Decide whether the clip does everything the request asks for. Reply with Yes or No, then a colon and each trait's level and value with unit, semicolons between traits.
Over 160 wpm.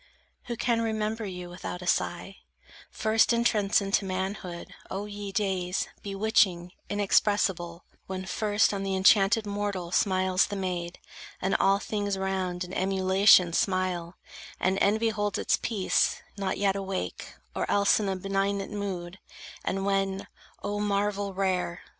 No: average, 140 wpm